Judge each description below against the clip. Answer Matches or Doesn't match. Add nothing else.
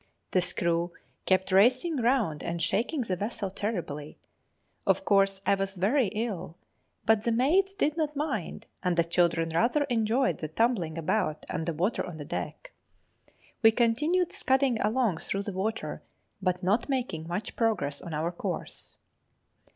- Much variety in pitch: Matches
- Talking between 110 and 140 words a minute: Doesn't match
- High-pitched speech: Matches